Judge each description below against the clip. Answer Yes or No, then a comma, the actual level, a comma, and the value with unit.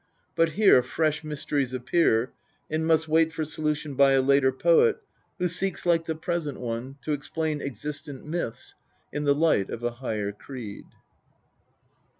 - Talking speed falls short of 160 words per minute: Yes, average, 150 wpm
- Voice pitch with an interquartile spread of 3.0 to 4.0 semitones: Yes, average, 3.7 semitones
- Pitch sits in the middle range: Yes, medium, 150 Hz